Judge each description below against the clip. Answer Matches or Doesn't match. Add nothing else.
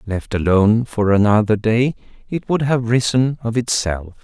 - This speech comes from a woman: Doesn't match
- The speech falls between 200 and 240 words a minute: Doesn't match